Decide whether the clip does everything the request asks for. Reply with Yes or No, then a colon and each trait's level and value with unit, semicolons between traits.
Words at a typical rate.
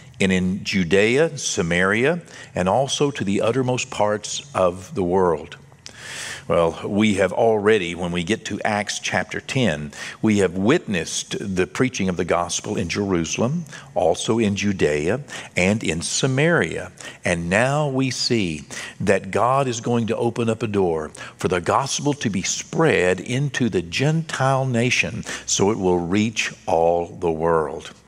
Yes: average, 150 wpm